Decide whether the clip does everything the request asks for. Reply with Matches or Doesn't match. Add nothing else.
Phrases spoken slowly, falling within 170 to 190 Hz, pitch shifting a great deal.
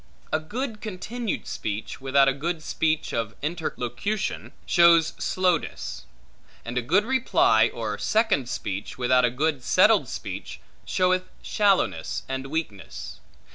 Doesn't match